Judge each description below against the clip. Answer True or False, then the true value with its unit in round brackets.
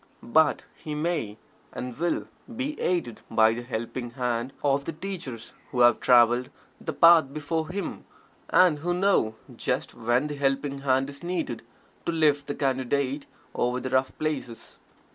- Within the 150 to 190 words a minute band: True (155 wpm)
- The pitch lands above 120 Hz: True (140 Hz)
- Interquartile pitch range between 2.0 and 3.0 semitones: False (4.4 semitones)